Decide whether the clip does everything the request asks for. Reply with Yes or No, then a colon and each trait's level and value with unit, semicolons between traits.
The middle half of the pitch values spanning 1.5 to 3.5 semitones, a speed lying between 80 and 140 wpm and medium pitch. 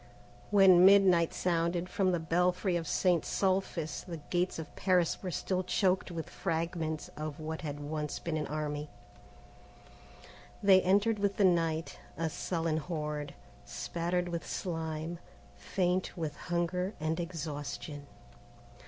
Yes: narrow, 2.6 semitones; slow, 135 wpm; medium, 170 Hz